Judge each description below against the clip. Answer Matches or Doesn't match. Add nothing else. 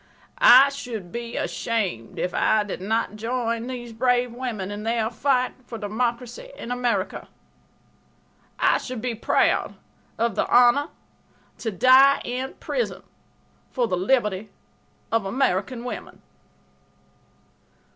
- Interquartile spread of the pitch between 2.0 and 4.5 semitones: Matches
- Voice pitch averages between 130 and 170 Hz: Doesn't match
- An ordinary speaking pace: Doesn't match